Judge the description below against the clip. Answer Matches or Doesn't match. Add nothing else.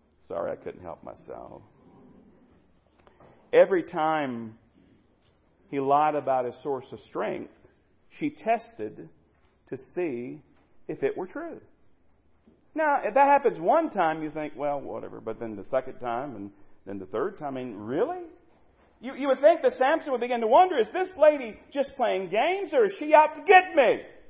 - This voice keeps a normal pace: Matches